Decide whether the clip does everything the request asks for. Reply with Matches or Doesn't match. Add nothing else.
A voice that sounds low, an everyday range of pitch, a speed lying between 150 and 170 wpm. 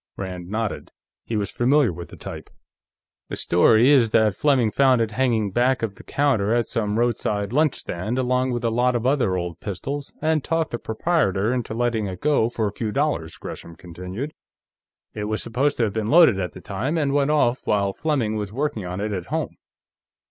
Doesn't match